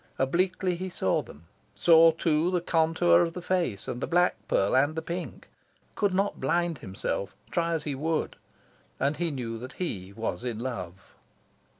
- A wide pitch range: Yes, wide, 6.2 semitones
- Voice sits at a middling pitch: Yes, medium, 160 Hz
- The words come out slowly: No, average, 175 wpm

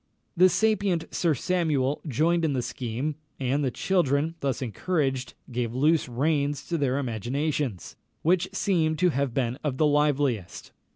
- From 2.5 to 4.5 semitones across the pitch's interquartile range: Yes, average, 4.2 semitones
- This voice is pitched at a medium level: Yes, medium, 145 Hz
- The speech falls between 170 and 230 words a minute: No, average, 150 wpm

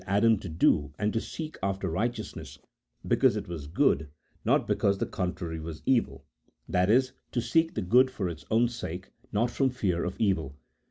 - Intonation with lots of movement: Yes, wide, 6.1 semitones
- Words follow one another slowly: No, average, 180 wpm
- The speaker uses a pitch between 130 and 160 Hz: No, low, 100 Hz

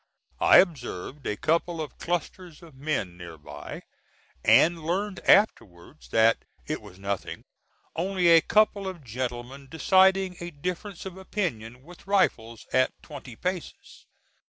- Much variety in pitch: Yes, wide, 7.3 semitones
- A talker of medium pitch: Yes, medium, 155 Hz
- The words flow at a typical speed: No, slow, 130 wpm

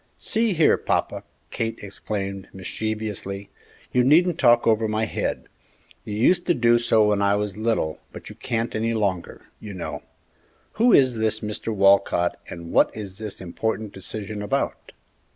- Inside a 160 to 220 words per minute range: No, average, 150 wpm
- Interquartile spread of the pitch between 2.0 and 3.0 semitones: Yes, average, 2.7 semitones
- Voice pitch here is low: Yes, low, 110 Hz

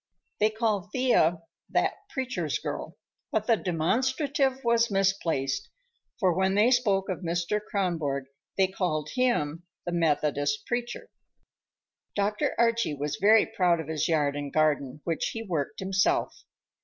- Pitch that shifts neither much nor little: No, wide, 6.2 semitones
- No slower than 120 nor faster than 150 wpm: Yes, slow, 135 wpm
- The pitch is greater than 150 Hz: Yes, medium, 185 Hz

